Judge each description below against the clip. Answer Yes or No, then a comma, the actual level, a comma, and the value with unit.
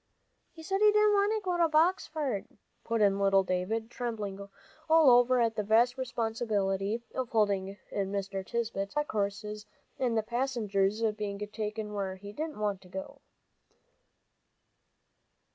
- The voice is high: Yes, high, 220 Hz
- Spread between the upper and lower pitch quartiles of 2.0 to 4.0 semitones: No, average, 4.5 semitones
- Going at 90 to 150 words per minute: Yes, average, 145 wpm